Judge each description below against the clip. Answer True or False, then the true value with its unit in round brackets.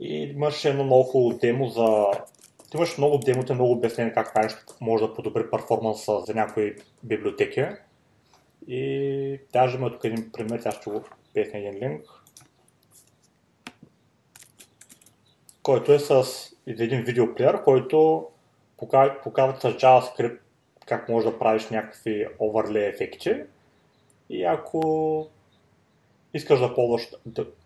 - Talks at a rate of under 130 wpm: True (115 wpm)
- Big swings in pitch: False (3.6 semitones)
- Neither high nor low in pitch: False (125 Hz)